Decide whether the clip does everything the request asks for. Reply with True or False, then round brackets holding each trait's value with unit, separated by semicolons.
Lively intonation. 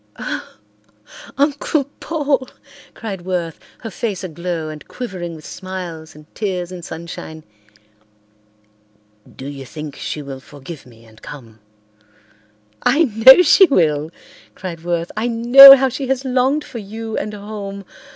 True (7.6 semitones)